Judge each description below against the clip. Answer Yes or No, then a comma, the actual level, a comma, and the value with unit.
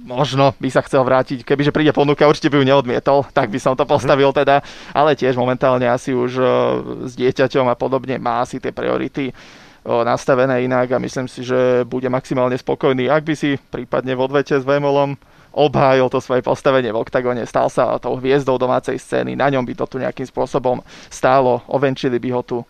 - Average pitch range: No, narrow, 1.9 semitones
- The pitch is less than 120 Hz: No, low, 130 Hz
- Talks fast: Yes, fast, 190 wpm